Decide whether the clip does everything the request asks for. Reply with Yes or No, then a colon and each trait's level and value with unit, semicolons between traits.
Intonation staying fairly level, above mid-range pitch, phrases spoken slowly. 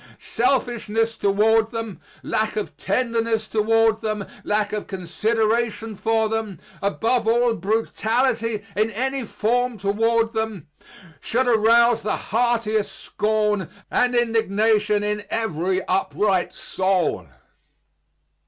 Yes: narrow, 1.7 semitones; high, 220 Hz; slow, 105 wpm